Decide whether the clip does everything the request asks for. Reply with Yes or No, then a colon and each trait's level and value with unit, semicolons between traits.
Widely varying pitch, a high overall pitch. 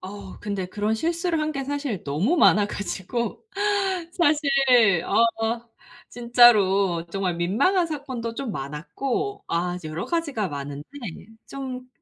Yes: wide, 7.0 semitones; high, 225 Hz